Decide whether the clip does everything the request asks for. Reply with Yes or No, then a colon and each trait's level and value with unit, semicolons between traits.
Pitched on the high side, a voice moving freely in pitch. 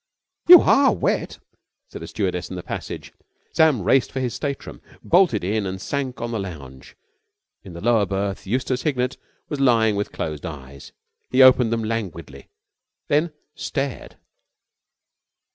No: low, 115 Hz; wide, 6.0 semitones